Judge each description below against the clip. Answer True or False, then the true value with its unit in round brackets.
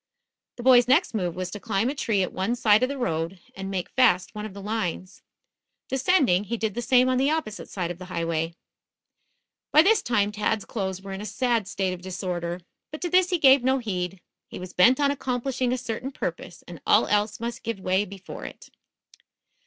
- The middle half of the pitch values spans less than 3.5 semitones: False (5.4 semitones)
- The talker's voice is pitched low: False (215 Hz)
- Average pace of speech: False (210 wpm)